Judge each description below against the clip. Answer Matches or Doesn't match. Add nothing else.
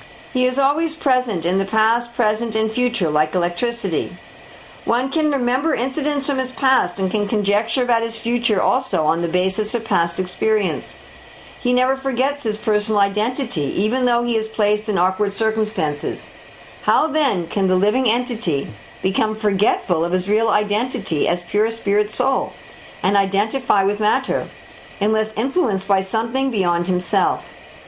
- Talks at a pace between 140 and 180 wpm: Matches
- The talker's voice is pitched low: Doesn't match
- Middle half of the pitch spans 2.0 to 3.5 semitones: Doesn't match